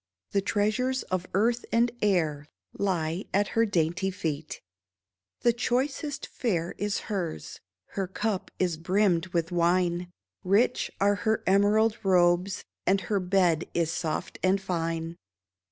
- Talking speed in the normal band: No, slow, 130 wpm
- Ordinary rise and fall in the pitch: Yes, average, 3.3 semitones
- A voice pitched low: No, high, 190 Hz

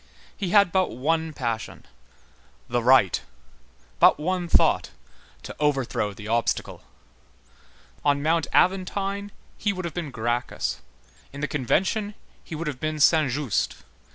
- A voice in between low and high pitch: Yes, medium, 155 Hz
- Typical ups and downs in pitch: No, wide, 6.2 semitones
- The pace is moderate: No, slow, 125 wpm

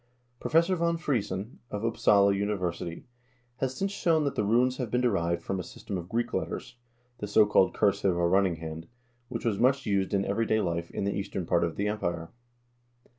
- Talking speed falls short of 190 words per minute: No, average, 200 wpm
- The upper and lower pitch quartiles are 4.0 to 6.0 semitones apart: Yes, average, 5.0 semitones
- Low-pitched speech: Yes, low, 100 Hz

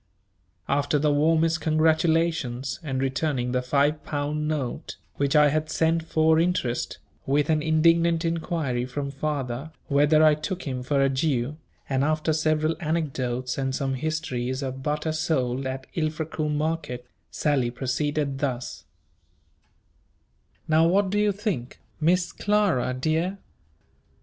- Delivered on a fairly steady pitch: No, average, 3.2 semitones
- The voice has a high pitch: No, medium, 150 Hz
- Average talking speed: No, slow, 130 wpm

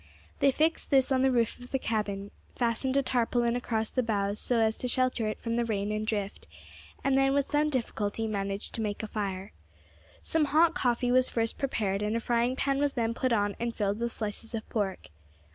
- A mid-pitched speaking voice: No, high, 230 Hz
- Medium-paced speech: No, fast, 210 wpm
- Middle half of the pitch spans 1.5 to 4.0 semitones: Yes, average, 3.4 semitones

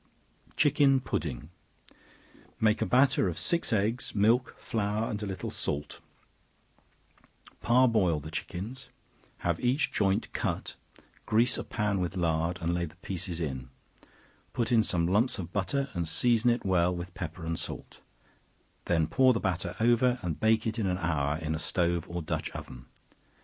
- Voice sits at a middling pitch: No, very low, 95 Hz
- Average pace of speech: Yes, average, 160 wpm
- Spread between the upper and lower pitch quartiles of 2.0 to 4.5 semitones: No, average, 5.3 semitones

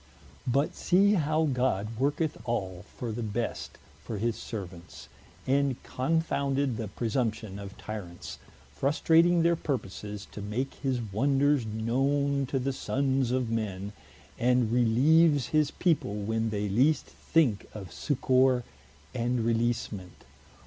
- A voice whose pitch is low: Yes, low, 125 Hz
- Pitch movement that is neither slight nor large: Yes, average, 4.6 semitones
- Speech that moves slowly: Yes, slow, 125 wpm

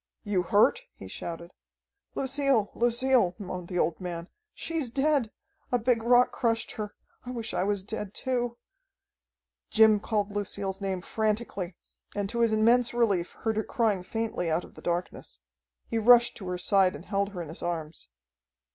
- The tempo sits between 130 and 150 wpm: No, average, 165 wpm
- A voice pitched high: Yes, high, 210 Hz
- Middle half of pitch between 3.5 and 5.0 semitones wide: Yes, average, 4.4 semitones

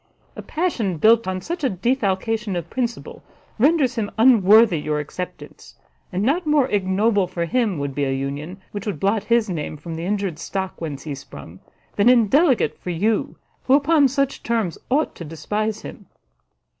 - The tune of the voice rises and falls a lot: Yes, wide, 5.7 semitones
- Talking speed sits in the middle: Yes, average, 170 wpm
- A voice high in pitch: Yes, high, 205 Hz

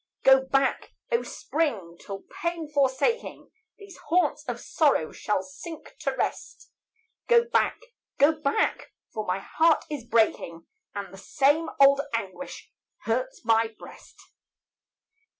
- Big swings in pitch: Yes, wide, 6.4 semitones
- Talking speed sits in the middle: No, slow, 125 wpm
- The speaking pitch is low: No, very high, 275 Hz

